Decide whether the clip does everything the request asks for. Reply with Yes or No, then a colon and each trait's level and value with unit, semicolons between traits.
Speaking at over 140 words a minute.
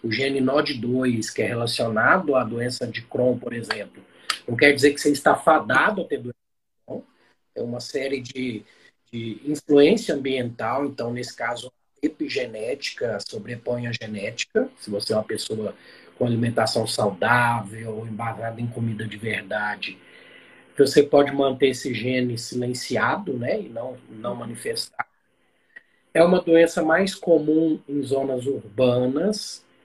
No: average, 135 wpm